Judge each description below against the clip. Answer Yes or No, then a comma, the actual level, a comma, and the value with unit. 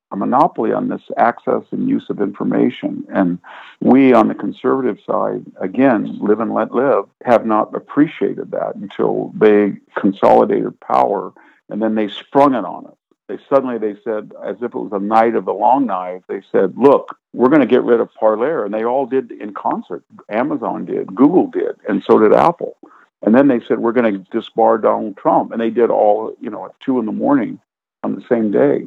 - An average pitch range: Yes, average, 4.8 semitones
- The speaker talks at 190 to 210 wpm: Yes, average, 200 wpm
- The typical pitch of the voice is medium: No, low, 115 Hz